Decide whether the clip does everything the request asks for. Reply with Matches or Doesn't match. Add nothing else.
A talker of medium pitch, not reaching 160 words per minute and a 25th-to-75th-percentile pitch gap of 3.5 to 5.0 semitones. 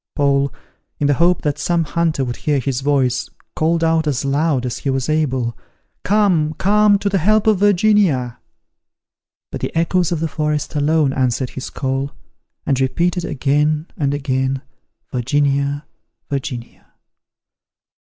Matches